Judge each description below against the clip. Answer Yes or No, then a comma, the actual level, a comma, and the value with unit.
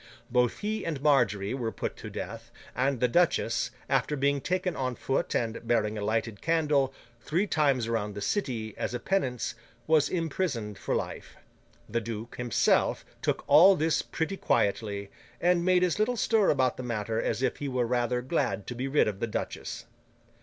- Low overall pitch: Yes, low, 125 Hz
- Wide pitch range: Yes, wide, 6.0 semitones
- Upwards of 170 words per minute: Yes, average, 180 wpm